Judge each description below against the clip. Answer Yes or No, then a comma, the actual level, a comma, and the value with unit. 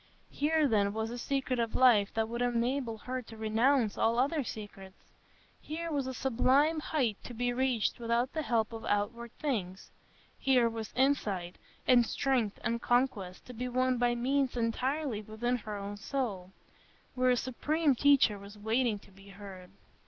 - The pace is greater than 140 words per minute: Yes, average, 165 wpm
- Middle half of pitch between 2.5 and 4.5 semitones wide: Yes, average, 3.3 semitones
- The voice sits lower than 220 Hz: No, high, 240 Hz